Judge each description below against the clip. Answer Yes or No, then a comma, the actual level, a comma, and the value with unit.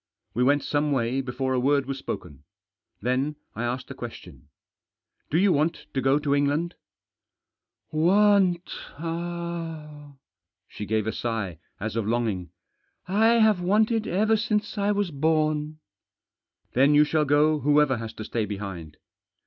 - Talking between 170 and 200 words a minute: No, average, 160 wpm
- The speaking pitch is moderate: Yes, medium, 145 Hz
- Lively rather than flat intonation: Yes, wide, 6.4 semitones